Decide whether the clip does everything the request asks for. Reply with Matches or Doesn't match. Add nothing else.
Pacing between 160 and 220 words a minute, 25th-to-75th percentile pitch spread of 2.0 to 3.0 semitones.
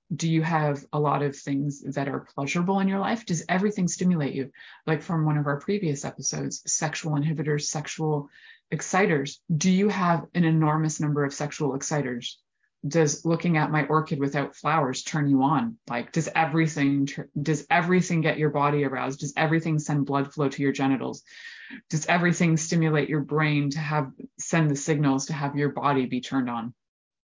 Matches